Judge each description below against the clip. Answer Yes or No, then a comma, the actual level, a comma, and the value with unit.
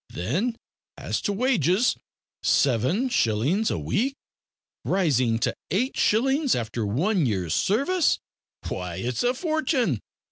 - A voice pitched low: No, high, 190 Hz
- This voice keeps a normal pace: No, slow, 115 wpm